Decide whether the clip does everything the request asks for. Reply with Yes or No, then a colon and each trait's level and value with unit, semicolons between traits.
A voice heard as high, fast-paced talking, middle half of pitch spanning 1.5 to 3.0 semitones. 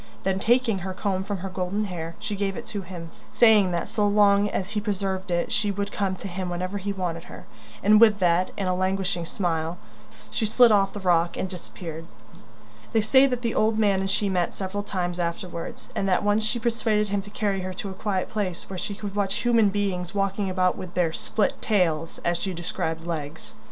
Yes: high, 195 Hz; fast, 215 wpm; narrow, 2.4 semitones